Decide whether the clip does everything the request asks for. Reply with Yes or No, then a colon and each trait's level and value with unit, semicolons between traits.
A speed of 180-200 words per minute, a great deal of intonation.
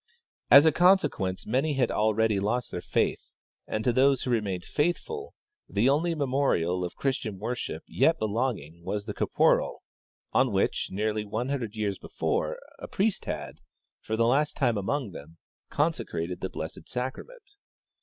No: average, 160 wpm; wide, 5.7 semitones